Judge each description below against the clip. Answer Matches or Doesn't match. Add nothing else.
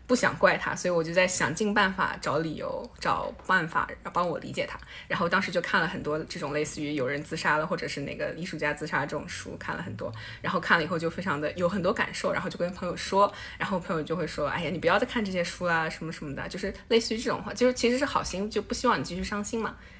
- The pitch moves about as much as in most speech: Matches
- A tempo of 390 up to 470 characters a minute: Matches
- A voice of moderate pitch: Matches